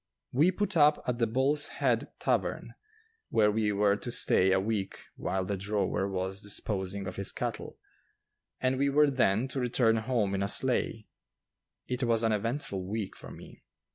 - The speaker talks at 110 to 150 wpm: No, average, 170 wpm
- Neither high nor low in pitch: No, low, 110 Hz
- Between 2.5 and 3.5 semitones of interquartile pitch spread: No, average, 4.6 semitones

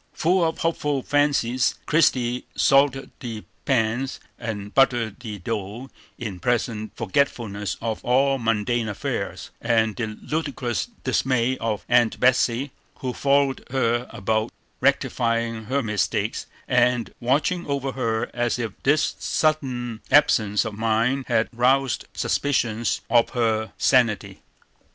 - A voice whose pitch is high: No, low, 120 Hz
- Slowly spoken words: Yes, slow, 120 wpm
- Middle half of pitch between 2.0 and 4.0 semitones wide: Yes, average, 3.3 semitones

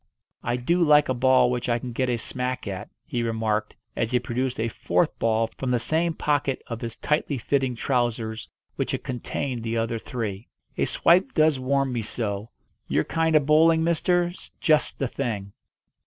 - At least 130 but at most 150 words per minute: No, average, 185 wpm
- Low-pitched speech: Yes, low, 125 Hz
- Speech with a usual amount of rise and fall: Yes, average, 4.3 semitones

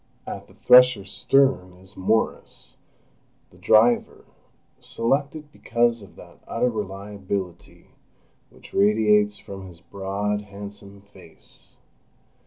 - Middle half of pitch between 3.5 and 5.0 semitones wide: No, average, 2.9 semitones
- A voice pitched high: No, low, 105 Hz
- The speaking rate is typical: No, slow, 100 wpm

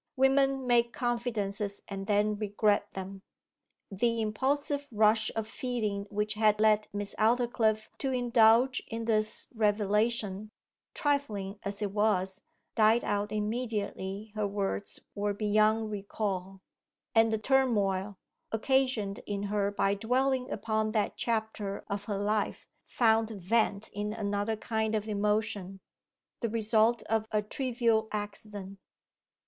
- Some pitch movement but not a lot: No, narrow, 2.0 semitones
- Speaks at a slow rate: Yes, slow, 125 wpm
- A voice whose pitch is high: Yes, high, 215 Hz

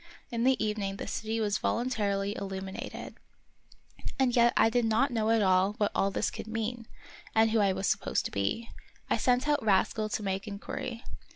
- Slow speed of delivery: No, average, 190 wpm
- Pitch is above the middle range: Yes, high, 220 Hz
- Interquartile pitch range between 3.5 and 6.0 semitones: No, average, 2.8 semitones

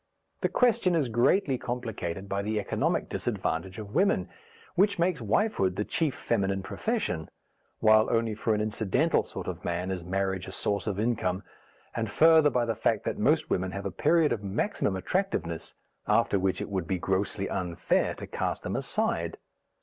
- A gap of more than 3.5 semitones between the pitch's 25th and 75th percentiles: Yes, wide, 5.4 semitones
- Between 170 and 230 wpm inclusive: Yes, average, 175 wpm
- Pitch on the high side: No, low, 105 Hz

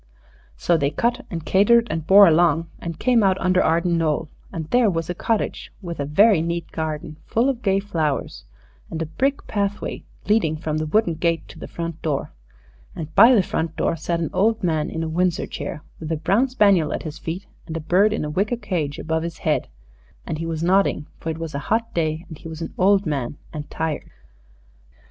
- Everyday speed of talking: No, fast, 215 wpm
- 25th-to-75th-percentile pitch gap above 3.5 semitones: Yes, average, 3.9 semitones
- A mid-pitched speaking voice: Yes, medium, 165 Hz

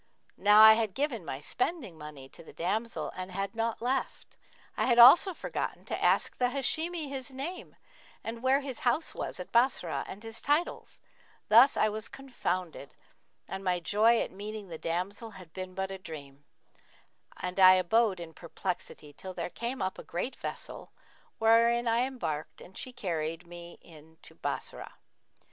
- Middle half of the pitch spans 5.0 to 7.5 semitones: Yes, wide, 5.5 semitones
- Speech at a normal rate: Yes, average, 165 wpm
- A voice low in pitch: No, high, 210 Hz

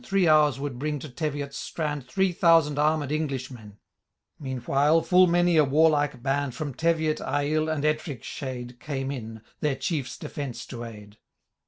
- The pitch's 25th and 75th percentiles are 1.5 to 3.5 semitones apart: Yes, average, 3.0 semitones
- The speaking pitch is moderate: Yes, medium, 145 Hz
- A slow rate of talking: No, average, 160 wpm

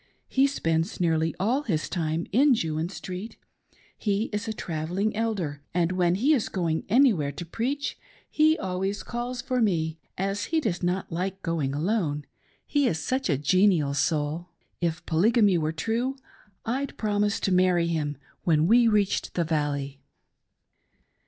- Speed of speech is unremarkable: Yes, average, 150 wpm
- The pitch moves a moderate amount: No, wide, 5.7 semitones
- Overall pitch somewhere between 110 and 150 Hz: No, medium, 185 Hz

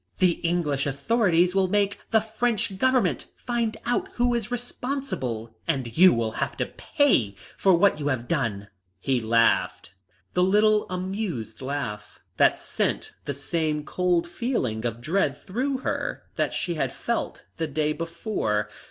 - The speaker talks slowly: No, average, 150 wpm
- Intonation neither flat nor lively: No, wide, 8.5 semitones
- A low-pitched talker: No, medium, 170 Hz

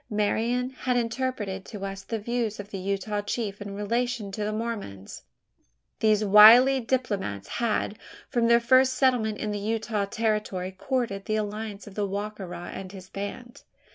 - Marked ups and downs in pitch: No, average, 2.9 semitones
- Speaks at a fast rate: No, average, 165 wpm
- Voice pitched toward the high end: Yes, high, 215 Hz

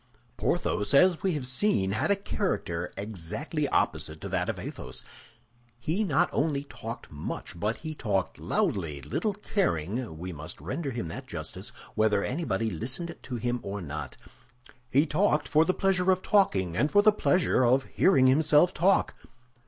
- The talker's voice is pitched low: Yes, low, 130 Hz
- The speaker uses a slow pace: No, average, 160 wpm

